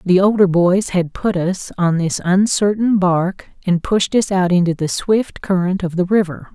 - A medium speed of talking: Yes, average, 190 wpm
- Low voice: No, medium, 185 Hz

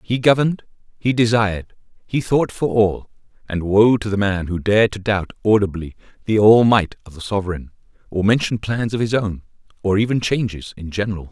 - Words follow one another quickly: No, average, 185 wpm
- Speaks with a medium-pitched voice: No, low, 105 Hz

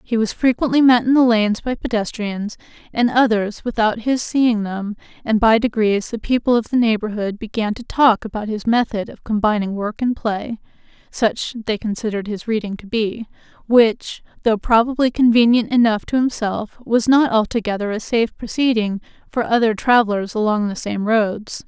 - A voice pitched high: Yes, high, 225 Hz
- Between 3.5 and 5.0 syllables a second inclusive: Yes, 4.6 syllables/s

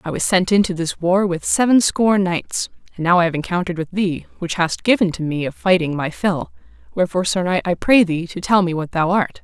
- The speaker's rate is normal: No, fast, 240 wpm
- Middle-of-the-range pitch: Yes, medium, 180 Hz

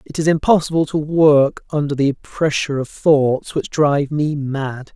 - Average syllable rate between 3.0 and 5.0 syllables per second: Yes, 4.4 syllables/s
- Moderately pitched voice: Yes, medium, 145 Hz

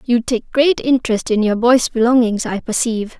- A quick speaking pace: No, average, 190 wpm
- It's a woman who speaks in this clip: Yes, female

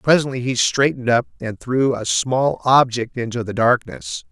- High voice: No, low, 125 Hz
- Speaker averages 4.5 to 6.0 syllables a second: Yes, 4.7 syllables/s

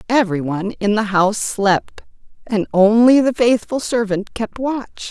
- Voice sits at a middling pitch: No, high, 215 Hz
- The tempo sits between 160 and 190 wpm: No, average, 140 wpm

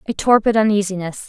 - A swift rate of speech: No, average, 140 wpm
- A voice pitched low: No, high, 205 Hz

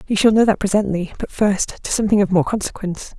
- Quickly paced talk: Yes, fast, 225 wpm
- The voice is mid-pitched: No, high, 200 Hz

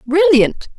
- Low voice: No, very high, 310 Hz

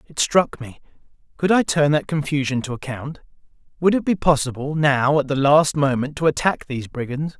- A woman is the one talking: No, male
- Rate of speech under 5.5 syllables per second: Yes, 5.3 syllables/s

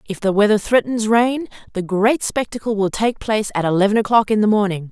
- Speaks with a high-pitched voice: Yes, high, 210 Hz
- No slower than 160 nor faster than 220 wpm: Yes, fast, 205 wpm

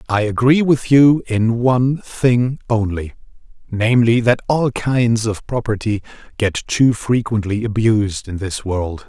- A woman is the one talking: No, male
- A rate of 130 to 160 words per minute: Yes, average, 140 wpm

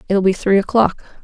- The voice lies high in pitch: Yes, high, 200 Hz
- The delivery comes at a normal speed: Yes, average, 195 wpm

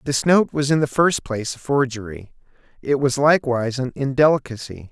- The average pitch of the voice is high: No, low, 135 Hz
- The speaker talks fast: No, average, 170 wpm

